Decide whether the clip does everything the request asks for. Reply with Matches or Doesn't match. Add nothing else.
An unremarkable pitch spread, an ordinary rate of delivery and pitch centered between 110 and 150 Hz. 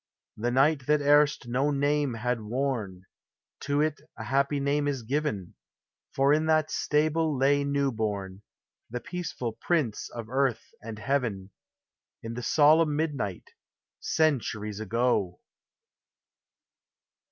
Doesn't match